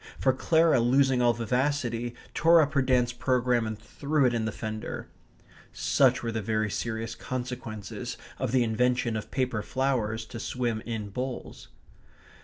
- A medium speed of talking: Yes, average, 155 wpm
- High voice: No, low, 120 Hz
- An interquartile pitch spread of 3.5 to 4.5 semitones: No, average, 2.7 semitones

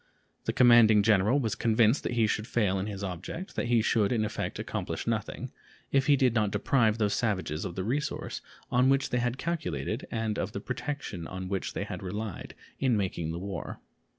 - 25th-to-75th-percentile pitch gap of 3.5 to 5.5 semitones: Yes, average, 3.8 semitones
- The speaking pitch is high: No, low, 110 Hz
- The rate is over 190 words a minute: Yes, average, 200 wpm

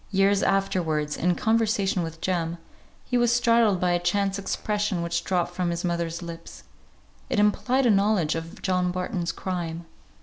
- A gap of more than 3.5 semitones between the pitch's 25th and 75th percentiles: No, average, 3.2 semitones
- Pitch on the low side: No, medium, 180 Hz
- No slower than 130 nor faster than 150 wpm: No, average, 160 wpm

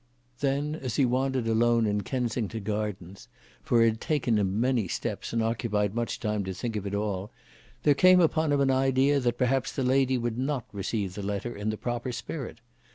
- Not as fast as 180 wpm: No, average, 200 wpm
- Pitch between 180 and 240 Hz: No, low, 120 Hz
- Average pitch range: Yes, average, 3.9 semitones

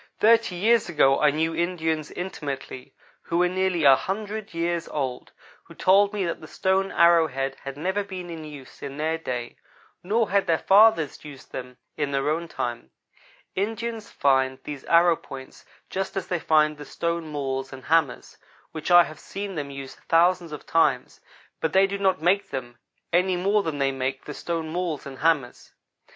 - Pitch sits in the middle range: Yes, medium, 165 Hz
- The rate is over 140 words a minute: Yes, average, 180 wpm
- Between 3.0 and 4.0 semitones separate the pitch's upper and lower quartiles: No, average, 5.1 semitones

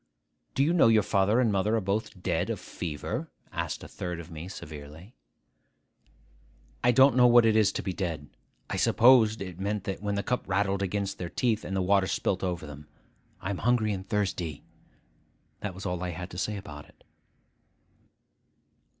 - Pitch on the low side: Yes, low, 100 Hz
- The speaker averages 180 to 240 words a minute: Yes, average, 185 wpm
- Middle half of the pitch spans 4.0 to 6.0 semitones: No, average, 3.3 semitones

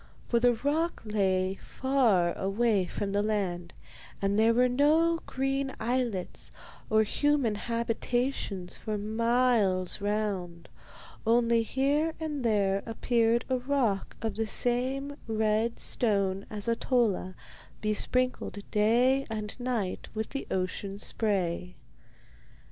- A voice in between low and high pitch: No, high, 225 Hz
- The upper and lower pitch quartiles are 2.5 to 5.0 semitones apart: Yes, average, 3.9 semitones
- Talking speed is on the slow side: Yes, slow, 115 wpm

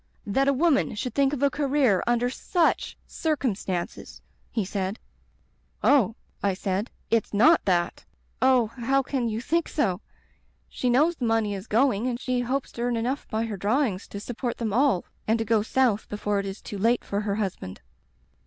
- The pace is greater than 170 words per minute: Yes, average, 190 wpm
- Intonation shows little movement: No, average, 4.5 semitones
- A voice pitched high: Yes, high, 230 Hz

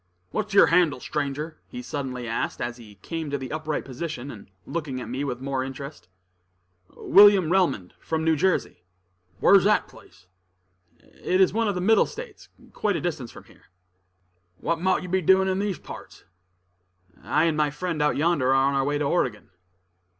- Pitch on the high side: No, medium, 155 Hz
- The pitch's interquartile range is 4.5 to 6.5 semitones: Yes, wide, 5.6 semitones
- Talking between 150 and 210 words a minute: Yes, average, 180 wpm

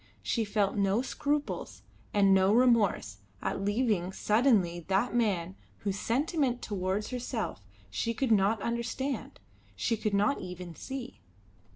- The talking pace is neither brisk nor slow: No, slow, 130 wpm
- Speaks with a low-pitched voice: No, high, 215 Hz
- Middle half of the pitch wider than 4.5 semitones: No, average, 3.9 semitones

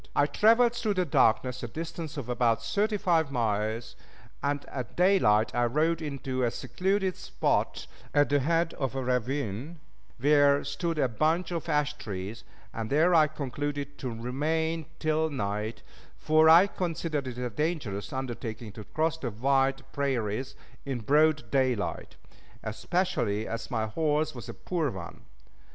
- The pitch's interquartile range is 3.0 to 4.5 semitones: No, average, 5.1 semitones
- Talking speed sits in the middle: Yes, average, 150 wpm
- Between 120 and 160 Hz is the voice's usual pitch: Yes, medium, 140 Hz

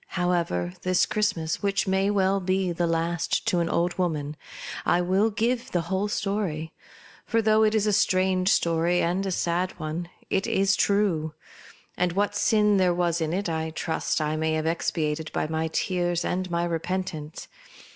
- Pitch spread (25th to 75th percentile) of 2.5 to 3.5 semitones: Yes, average, 2.9 semitones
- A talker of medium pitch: Yes, medium, 175 Hz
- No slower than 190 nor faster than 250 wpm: No, average, 170 wpm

